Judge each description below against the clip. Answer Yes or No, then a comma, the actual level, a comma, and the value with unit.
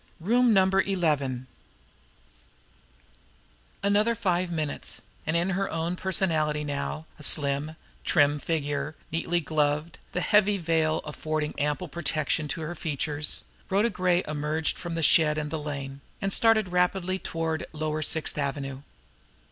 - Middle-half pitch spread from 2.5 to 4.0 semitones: Yes, average, 3.3 semitones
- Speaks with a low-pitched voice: No, medium, 160 Hz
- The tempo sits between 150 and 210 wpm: No, slow, 135 wpm